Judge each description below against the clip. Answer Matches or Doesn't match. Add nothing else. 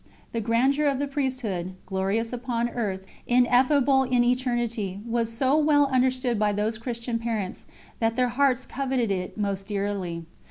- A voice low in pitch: Doesn't match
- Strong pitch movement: Doesn't match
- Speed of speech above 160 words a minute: Doesn't match